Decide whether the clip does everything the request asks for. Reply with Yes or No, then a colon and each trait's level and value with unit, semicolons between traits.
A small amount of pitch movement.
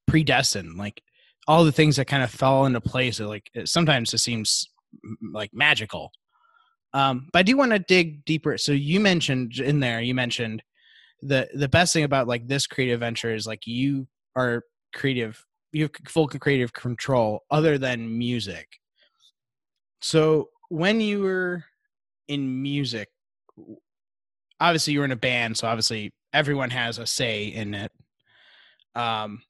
No: average, 5.0 semitones